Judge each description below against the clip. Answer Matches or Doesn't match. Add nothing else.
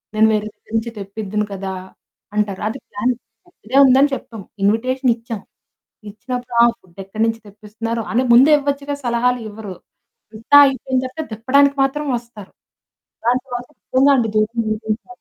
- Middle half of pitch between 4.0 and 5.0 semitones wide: Doesn't match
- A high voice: Matches